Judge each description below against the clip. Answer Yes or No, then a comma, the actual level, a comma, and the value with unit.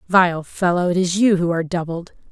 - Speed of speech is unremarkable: Yes, average, 180 wpm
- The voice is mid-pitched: Yes, medium, 175 Hz